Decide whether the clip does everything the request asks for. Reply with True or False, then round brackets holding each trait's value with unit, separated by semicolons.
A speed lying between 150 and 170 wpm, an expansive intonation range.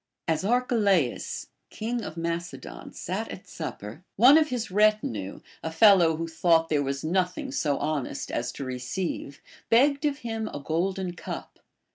True (160 wpm; 6.6 semitones)